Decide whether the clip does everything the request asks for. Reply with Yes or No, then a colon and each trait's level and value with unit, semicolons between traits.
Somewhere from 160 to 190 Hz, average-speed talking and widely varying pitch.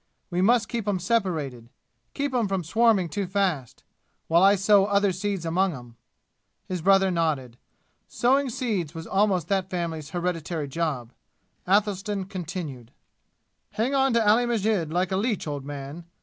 No: medium, 185 Hz; average, 150 wpm; average, 4.3 semitones